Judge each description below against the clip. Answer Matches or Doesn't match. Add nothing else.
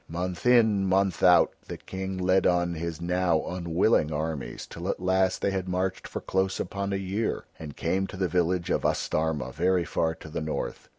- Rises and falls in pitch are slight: Matches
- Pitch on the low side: Matches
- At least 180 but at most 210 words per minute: Matches